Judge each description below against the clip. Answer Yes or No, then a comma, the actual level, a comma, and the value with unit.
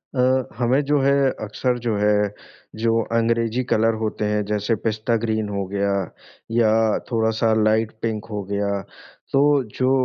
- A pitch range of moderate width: No, narrow, 2.0 semitones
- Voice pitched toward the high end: No, low, 110 Hz